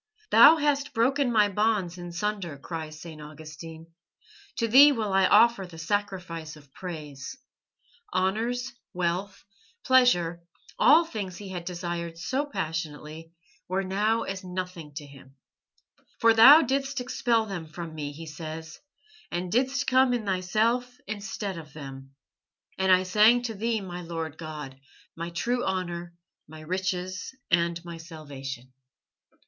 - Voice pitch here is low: No, medium, 185 Hz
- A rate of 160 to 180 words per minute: No, average, 140 wpm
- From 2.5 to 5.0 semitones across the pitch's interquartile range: No, wide, 5.5 semitones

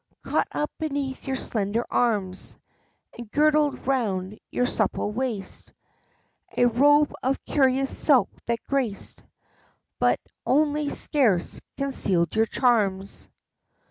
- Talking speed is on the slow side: Yes, slow, 110 wpm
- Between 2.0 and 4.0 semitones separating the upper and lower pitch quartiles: No, average, 4.8 semitones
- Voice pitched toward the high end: Yes, very high, 250 Hz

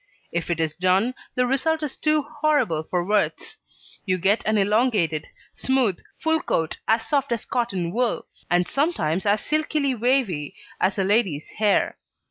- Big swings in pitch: Yes, wide, 6.8 semitones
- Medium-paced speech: Yes, average, 155 wpm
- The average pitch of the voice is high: Yes, high, 215 Hz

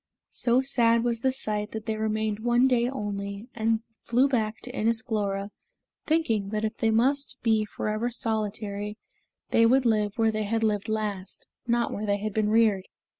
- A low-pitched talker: No, high, 220 Hz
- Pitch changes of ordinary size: No, narrow, 2.0 semitones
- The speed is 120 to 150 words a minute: No, average, 175 wpm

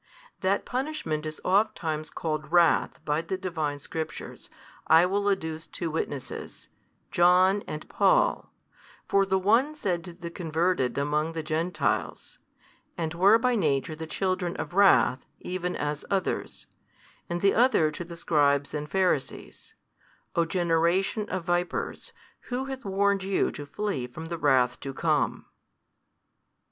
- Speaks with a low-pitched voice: No, medium, 170 Hz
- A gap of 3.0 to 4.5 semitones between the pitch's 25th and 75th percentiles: Yes, average, 3.9 semitones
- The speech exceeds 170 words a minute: No, average, 140 wpm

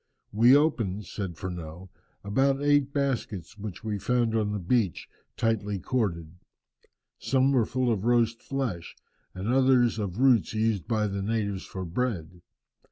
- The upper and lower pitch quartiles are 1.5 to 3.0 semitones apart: No, average, 4.6 semitones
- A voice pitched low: Yes, low, 110 Hz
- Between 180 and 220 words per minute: No, average, 145 wpm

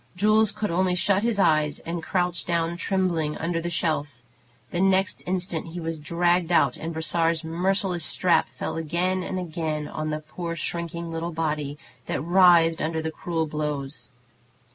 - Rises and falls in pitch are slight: Yes, narrow, 2.1 semitones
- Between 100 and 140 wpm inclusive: No, average, 165 wpm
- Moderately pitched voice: Yes, medium, 170 Hz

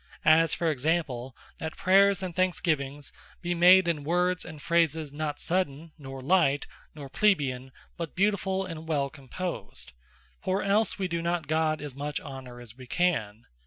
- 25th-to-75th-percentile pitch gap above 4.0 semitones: Yes, average, 4.4 semitones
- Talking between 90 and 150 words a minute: No, average, 160 wpm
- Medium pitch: Yes, medium, 160 Hz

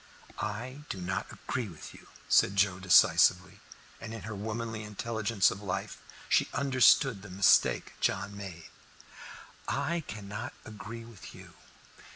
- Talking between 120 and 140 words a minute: Yes, slow, 135 wpm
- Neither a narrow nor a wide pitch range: Yes, average, 3.0 semitones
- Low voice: Yes, low, 105 Hz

